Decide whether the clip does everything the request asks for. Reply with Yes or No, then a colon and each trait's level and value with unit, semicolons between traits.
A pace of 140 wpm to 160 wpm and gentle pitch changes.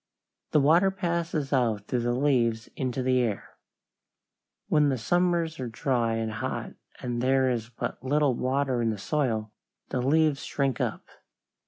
No: average, 155 wpm; average, 4.0 semitones